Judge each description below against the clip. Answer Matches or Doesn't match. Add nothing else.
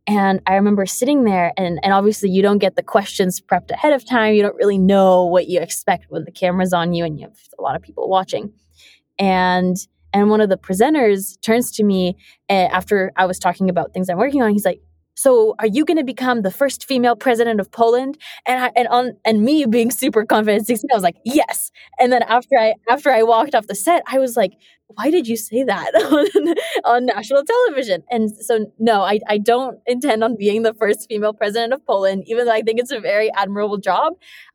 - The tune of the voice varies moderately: Matches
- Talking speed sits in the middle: Doesn't match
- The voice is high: Matches